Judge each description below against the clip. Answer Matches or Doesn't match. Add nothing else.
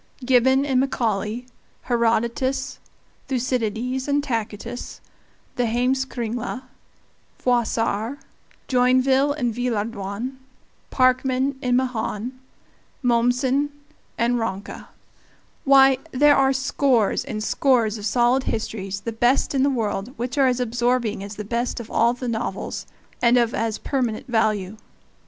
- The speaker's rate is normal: Doesn't match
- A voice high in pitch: Matches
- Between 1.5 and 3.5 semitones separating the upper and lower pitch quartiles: Matches